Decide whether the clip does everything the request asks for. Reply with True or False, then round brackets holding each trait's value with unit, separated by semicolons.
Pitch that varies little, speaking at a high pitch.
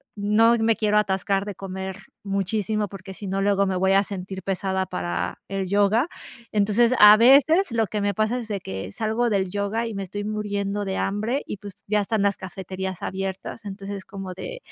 True (2.0 semitones; 200 Hz)